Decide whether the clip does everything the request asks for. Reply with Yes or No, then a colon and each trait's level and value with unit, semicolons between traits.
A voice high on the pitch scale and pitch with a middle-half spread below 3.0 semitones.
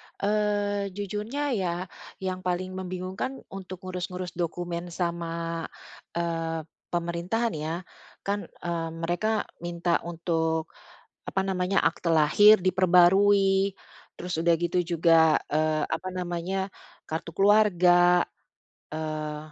No: medium, 180 Hz; narrow, 2.4 semitones